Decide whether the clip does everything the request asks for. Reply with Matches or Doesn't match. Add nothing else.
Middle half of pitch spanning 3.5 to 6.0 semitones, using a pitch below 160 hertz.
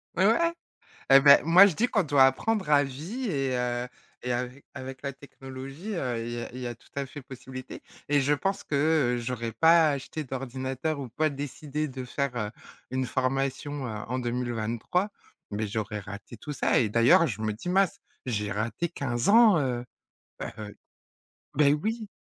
Matches